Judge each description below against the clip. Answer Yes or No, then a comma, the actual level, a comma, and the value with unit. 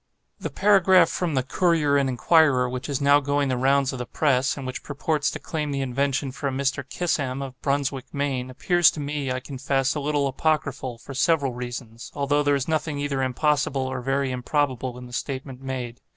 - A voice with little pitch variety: Yes, narrow, 2.1 semitones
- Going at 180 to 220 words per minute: Yes, average, 200 wpm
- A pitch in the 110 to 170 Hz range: Yes, medium, 140 Hz